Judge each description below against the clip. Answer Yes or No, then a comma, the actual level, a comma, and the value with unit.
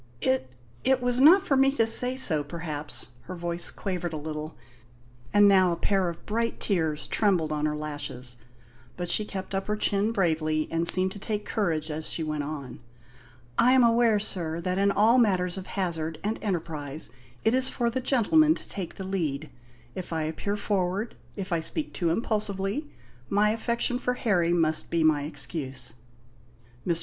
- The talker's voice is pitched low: No, medium, 185 Hz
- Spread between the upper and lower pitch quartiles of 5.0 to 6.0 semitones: Yes, average, 5.3 semitones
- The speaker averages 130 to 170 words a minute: No, average, 180 wpm